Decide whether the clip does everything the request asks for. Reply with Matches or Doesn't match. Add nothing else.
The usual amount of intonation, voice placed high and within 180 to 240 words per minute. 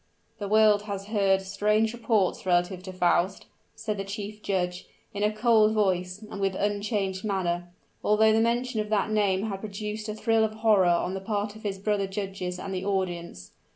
Doesn't match